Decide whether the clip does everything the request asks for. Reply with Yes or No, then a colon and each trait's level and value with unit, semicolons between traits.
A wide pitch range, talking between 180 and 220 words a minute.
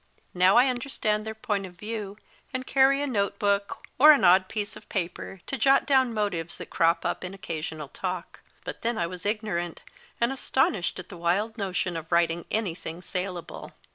No: average, 4.5 semitones; average, 185 wpm